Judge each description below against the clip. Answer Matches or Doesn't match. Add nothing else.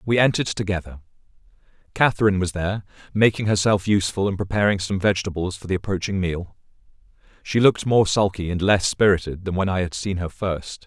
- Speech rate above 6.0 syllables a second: Matches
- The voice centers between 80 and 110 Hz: Matches